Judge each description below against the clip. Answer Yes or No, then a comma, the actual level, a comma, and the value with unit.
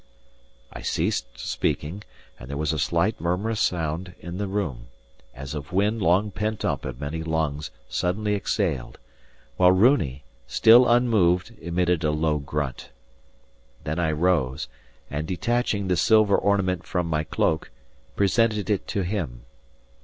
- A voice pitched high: No, very low, 90 Hz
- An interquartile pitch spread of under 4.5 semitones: No, average, 5.0 semitones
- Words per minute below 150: Yes, average, 140 wpm